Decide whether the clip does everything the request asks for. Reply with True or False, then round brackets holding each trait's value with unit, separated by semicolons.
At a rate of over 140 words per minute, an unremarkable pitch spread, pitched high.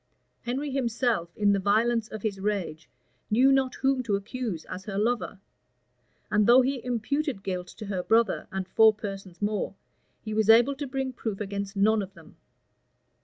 True (170 wpm; 3.9 semitones; 215 Hz)